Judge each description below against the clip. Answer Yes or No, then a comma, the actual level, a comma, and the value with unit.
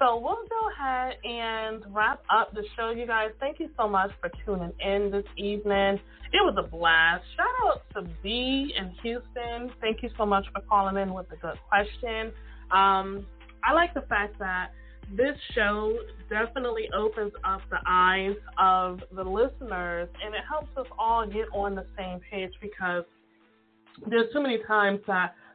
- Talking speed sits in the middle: Yes, average, 170 wpm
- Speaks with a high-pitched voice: Yes, high, 210 Hz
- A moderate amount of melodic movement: Yes, average, 4.1 semitones